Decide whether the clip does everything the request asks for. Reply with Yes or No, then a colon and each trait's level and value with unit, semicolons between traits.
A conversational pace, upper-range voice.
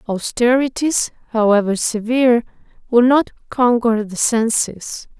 No: slow, 90 wpm; high, 235 Hz